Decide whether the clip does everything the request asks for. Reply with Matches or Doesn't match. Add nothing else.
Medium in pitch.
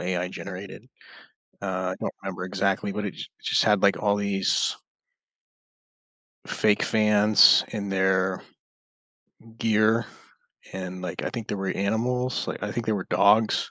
Doesn't match